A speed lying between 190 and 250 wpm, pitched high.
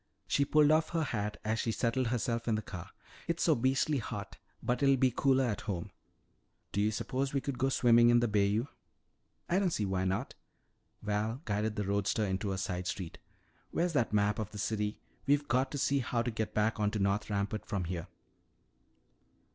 No: average, 200 wpm; low, 110 Hz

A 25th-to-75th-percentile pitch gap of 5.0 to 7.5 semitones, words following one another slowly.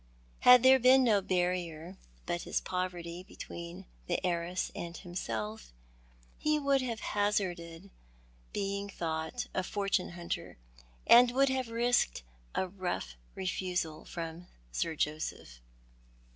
No: average, 3.7 semitones; slow, 115 wpm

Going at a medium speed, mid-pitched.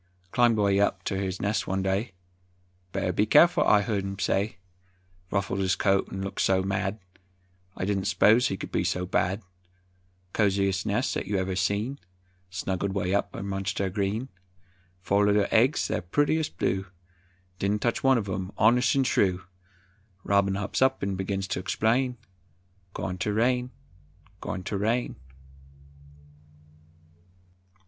No: average, 150 wpm; low, 100 Hz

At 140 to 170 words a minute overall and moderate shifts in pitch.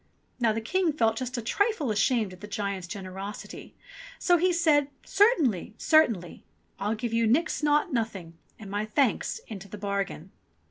No: average, 165 wpm; wide, 6.7 semitones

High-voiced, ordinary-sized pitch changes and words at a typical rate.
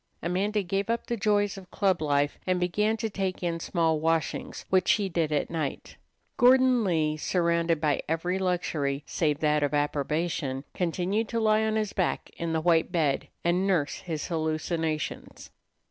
No: medium, 170 Hz; average, 3.9 semitones; average, 165 wpm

